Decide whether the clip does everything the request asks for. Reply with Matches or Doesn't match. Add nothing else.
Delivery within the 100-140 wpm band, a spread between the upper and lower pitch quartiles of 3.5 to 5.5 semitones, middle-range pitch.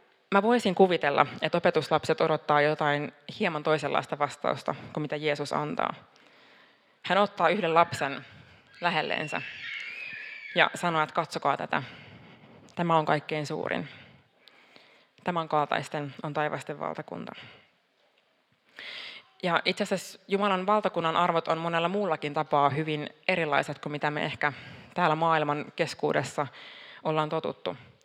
Doesn't match